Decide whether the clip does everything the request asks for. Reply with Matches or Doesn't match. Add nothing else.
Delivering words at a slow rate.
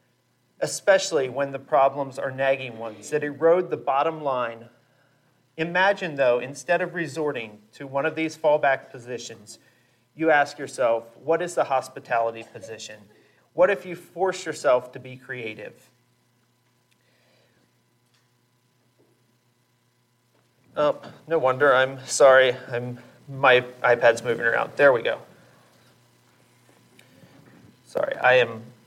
Matches